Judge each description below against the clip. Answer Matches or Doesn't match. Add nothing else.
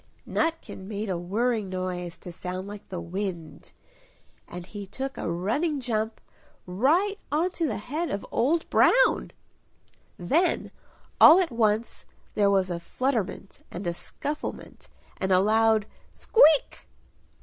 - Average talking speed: Doesn't match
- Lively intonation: Matches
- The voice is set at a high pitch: Matches